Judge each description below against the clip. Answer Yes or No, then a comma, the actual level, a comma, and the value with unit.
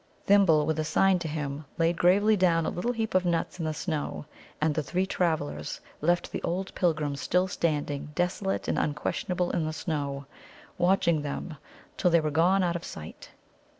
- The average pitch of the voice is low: No, medium, 165 Hz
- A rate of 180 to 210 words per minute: Yes, average, 185 wpm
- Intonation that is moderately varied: Yes, average, 3.2 semitones